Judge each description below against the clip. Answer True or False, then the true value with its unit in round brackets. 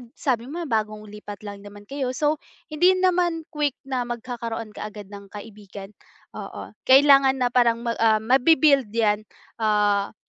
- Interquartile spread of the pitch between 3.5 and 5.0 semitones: True (4.6 semitones)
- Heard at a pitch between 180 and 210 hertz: False (235 Hz)